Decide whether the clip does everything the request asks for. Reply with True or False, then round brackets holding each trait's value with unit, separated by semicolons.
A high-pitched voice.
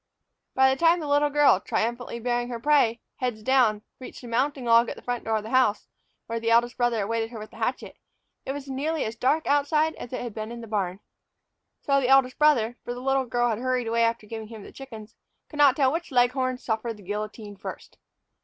True (245 Hz)